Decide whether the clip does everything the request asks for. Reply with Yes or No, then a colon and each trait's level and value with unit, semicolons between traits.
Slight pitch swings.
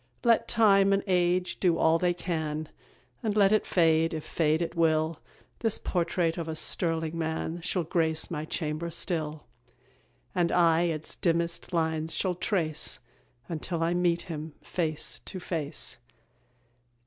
Yes: narrow, 2.0 semitones